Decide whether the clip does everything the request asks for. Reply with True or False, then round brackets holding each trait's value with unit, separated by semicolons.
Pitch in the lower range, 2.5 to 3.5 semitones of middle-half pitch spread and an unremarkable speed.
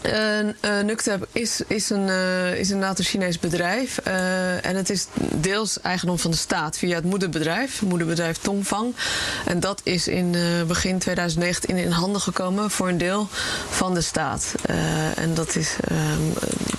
False (185 Hz; 2.8 semitones; 155 wpm)